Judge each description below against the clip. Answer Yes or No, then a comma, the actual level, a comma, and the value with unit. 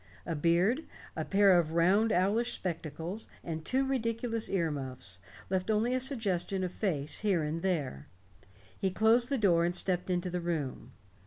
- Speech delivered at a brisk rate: No, average, 165 wpm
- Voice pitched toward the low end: No, medium, 185 Hz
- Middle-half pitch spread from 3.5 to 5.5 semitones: Yes, average, 4.8 semitones